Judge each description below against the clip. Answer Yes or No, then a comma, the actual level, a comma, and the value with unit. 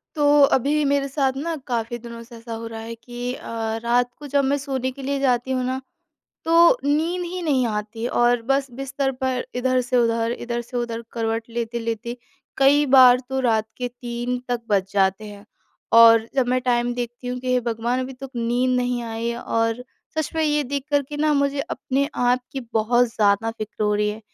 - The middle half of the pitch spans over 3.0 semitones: No, average, 2.7 semitones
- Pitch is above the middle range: Yes, high, 245 Hz